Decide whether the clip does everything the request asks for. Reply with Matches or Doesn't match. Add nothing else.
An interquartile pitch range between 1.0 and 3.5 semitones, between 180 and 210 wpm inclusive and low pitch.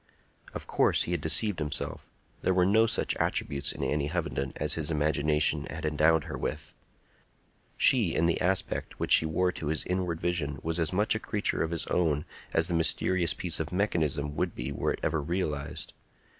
Matches